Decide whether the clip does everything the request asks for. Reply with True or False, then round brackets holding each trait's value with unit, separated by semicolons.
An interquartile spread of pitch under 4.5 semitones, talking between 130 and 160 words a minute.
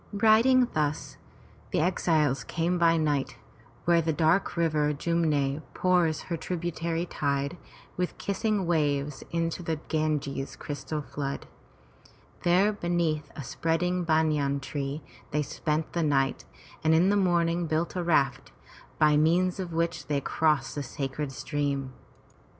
True (2.9 semitones; 135 wpm)